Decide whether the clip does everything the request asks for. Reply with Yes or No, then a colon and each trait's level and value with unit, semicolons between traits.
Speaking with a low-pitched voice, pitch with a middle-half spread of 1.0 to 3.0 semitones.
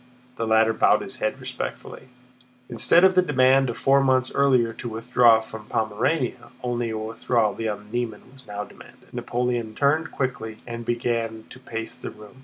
Yes: low, 120 Hz; narrow, 2.5 semitones